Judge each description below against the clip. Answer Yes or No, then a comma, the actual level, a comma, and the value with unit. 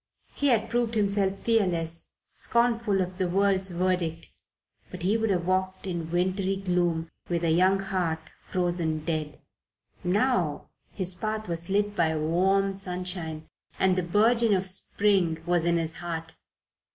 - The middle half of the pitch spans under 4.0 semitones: Yes, average, 2.7 semitones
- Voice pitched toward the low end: No, medium, 185 Hz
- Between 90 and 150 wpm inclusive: Yes, average, 145 wpm